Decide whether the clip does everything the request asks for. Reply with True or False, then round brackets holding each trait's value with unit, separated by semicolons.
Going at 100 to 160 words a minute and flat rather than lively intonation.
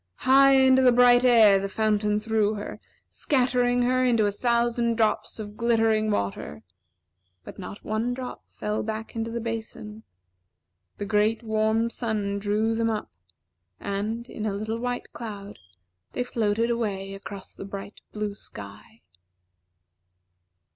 True (140 wpm; 2.3 semitones)